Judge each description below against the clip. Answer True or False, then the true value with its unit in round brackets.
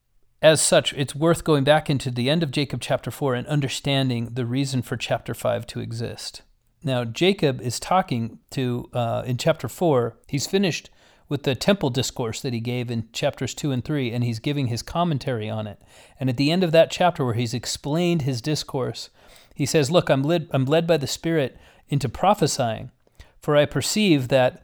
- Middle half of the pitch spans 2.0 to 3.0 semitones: False (3.9 semitones)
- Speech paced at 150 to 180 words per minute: False (195 wpm)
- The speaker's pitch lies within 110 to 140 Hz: True (135 Hz)